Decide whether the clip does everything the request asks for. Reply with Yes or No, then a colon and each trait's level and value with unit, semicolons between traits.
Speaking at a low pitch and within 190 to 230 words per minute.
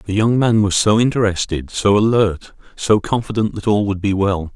Yes: low, 100 Hz; average, 200 wpm